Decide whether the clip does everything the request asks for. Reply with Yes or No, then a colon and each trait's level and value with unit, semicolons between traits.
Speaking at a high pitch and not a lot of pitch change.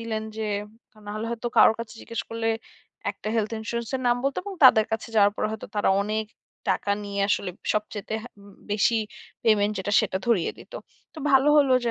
Yes: high, 220 Hz; narrow, 2.2 semitones